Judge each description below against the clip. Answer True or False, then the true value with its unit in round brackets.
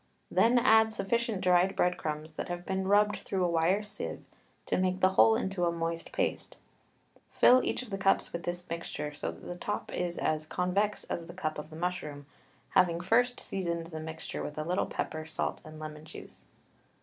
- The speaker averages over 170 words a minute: True (195 wpm)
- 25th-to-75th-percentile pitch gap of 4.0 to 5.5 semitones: False (3.2 semitones)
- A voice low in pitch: False (180 Hz)